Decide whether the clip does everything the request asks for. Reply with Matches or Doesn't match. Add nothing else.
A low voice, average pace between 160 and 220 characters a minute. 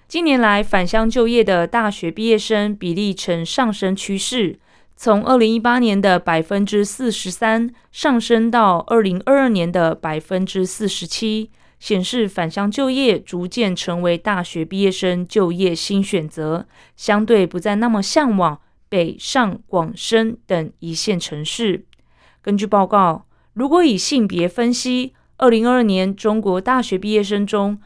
Doesn't match